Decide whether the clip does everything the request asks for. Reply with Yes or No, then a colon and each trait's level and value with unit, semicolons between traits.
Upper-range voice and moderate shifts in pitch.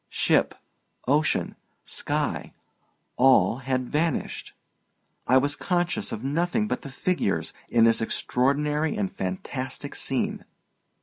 No: low, 135 Hz; average, 4.4 semitones